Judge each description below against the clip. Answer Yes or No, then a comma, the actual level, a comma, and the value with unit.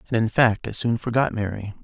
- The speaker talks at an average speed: No, fast, 230 wpm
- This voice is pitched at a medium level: No, low, 115 Hz